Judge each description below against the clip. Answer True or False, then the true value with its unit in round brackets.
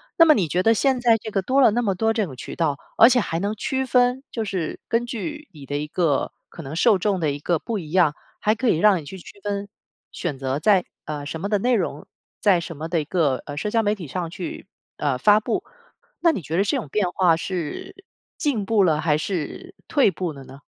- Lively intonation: True (6.0 semitones)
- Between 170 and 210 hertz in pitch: True (190 Hz)